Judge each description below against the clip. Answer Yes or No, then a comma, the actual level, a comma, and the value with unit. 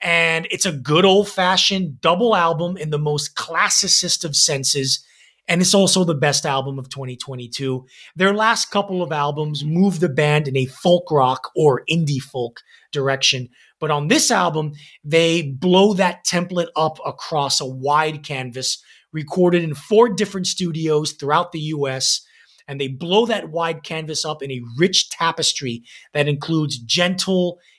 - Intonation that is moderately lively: Yes, average, 4.2 semitones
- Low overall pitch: No, medium, 155 Hz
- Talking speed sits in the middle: Yes, average, 160 wpm